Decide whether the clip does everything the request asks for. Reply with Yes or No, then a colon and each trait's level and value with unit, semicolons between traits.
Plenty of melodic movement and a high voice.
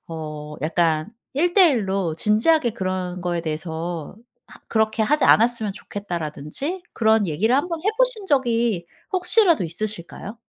Yes: wide, 8.4 semitones; high, 210 Hz